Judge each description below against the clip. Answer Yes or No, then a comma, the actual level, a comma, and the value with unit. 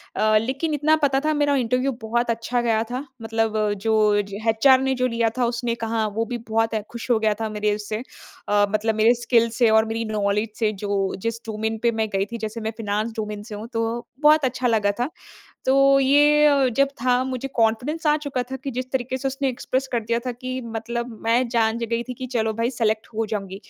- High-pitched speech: Yes, high, 230 Hz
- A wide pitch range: No, average, 2.7 semitones